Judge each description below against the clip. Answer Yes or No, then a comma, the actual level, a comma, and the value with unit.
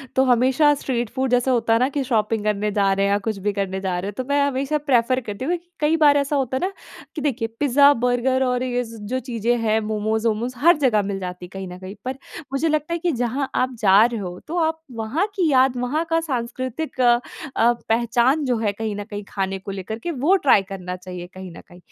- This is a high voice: Yes, high, 240 Hz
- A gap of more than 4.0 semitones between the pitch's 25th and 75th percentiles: Yes, average, 4.6 semitones